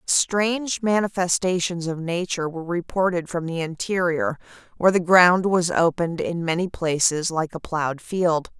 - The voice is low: No, medium, 175 Hz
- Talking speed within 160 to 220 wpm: No, average, 145 wpm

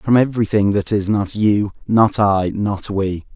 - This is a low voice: Yes, low, 105 Hz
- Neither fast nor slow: Yes, average, 180 wpm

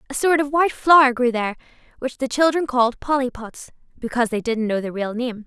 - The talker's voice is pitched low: No, very high, 255 Hz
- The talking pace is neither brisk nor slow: No, fast, 210 wpm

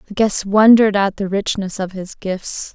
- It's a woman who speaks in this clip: Yes, female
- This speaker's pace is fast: No, average, 195 wpm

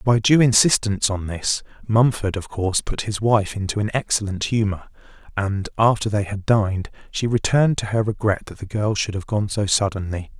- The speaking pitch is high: No, low, 105 Hz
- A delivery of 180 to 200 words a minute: Yes, average, 190 wpm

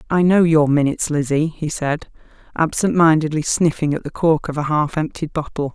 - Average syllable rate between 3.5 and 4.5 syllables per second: No, 5.3 syllables/s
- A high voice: No, medium, 155 Hz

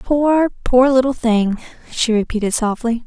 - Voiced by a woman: Yes, female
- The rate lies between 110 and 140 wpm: Yes, slow, 135 wpm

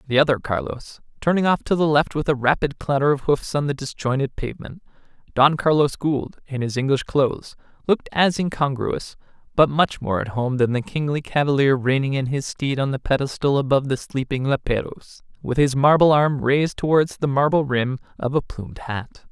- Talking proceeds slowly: No, average, 185 wpm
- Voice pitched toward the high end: No, medium, 140 Hz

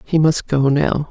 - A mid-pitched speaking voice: Yes, medium, 150 Hz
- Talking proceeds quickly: Yes, fast, 215 wpm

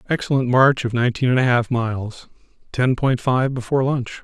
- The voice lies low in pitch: Yes, low, 125 Hz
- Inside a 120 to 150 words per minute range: No, average, 185 wpm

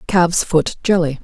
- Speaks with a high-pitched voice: No, medium, 170 Hz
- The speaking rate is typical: Yes, average, 145 wpm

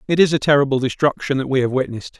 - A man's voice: Yes, male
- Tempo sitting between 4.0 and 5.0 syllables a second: No, 7.4 syllables/s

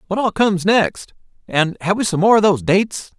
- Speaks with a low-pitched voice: No, high, 190 Hz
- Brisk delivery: Yes, fast, 225 wpm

